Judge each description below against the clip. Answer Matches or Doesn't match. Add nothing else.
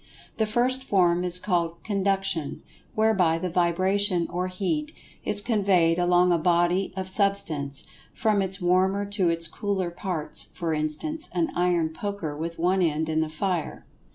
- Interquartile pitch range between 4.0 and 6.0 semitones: Doesn't match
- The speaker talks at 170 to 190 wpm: Doesn't match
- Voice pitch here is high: Doesn't match